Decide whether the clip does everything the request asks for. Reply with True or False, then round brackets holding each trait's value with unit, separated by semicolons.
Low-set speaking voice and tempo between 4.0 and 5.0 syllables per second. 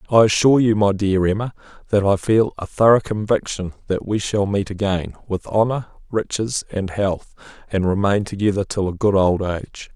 False (100 Hz; 5.2 syllables/s)